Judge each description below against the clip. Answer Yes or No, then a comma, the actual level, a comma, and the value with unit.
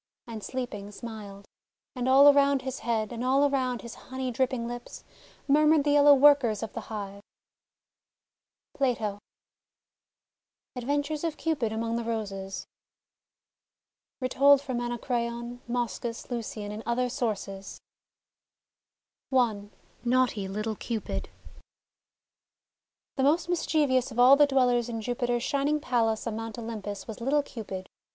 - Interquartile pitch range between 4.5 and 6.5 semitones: No, average, 3.4 semitones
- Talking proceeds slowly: Yes, slow, 125 wpm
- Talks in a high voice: Yes, high, 240 Hz